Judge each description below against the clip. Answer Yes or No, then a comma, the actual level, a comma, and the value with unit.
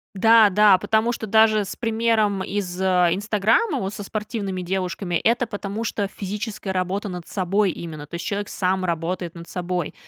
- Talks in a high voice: Yes, high, 195 Hz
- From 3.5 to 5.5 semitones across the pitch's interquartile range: No, average, 2.8 semitones